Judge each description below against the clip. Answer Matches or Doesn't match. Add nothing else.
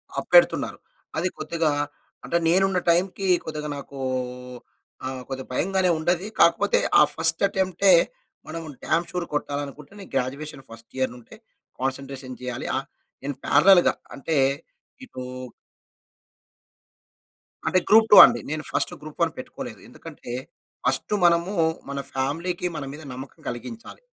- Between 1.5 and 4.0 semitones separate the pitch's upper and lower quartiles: Doesn't match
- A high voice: Doesn't match